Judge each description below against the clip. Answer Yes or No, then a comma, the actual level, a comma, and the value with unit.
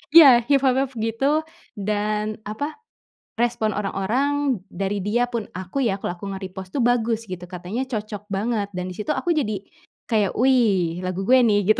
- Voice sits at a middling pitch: No, high, 215 Hz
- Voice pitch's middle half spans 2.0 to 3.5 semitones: No, average, 4.2 semitones